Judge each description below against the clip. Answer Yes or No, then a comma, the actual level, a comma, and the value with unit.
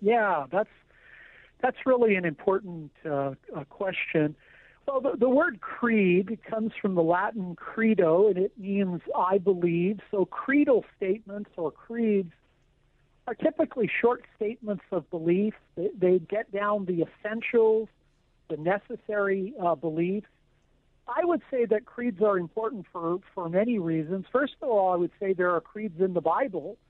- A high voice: Yes, high, 200 Hz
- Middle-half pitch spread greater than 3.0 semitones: Yes, average, 3.9 semitones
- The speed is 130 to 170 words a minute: Yes, average, 150 wpm